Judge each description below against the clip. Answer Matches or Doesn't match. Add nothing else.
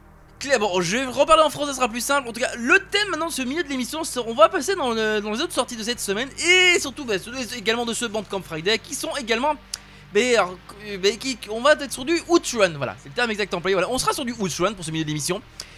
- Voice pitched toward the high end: Matches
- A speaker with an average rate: Doesn't match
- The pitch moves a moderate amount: Doesn't match